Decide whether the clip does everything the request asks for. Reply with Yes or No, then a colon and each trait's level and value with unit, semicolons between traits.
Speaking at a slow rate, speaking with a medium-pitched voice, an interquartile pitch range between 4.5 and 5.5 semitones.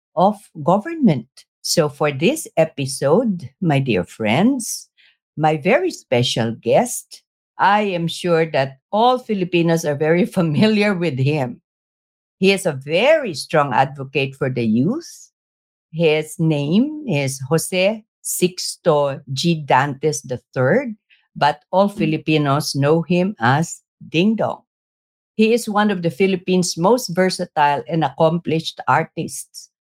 Yes: slow, 115 wpm; medium, 165 Hz; average, 5.1 semitones